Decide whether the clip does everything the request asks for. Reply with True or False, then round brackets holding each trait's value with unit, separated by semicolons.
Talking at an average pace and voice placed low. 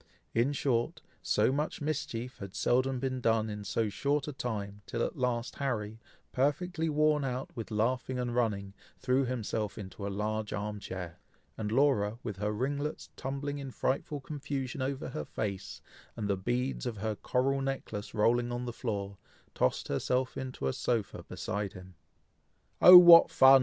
True (165 wpm; 120 Hz)